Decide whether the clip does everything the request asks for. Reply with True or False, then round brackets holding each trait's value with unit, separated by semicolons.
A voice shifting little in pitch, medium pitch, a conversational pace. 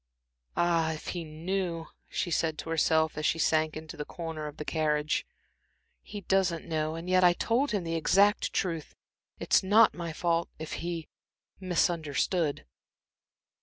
True (2.2 semitones; 165 Hz; 155 wpm)